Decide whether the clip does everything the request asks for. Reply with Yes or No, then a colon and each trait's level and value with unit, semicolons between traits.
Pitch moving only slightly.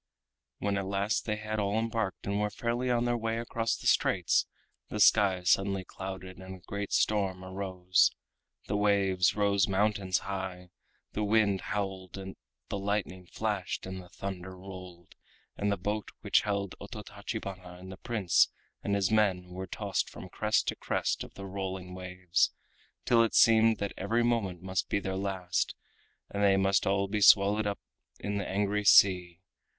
Yes: narrow, 1.9 semitones